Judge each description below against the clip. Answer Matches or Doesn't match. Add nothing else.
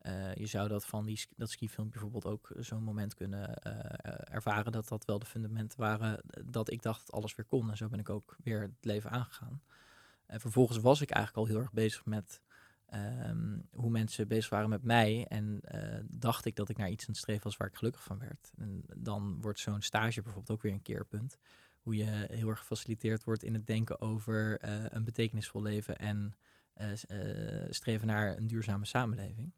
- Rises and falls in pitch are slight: Matches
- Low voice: Matches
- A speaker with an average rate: Doesn't match